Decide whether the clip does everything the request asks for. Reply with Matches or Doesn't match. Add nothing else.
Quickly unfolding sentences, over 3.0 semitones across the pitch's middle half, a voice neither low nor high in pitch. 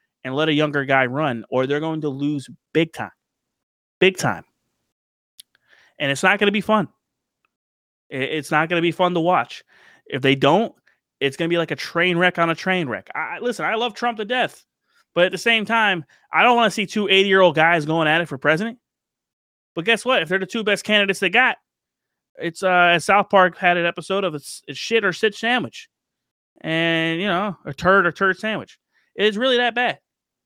Matches